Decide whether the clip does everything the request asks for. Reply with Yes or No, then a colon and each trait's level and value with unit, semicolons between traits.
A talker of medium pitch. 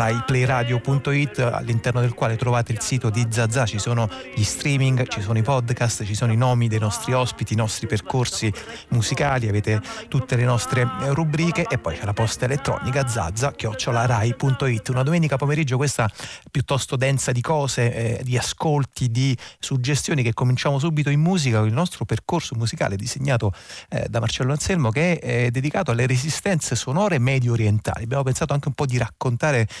No: low, 125 Hz